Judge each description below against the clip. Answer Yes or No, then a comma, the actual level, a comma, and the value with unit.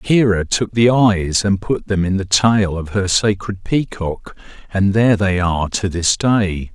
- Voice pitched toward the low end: Yes, low, 100 Hz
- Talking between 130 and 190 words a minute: Yes, average, 185 wpm